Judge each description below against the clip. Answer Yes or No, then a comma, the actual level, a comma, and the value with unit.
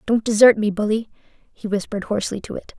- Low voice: No, high, 215 Hz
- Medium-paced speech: Yes, average, 195 wpm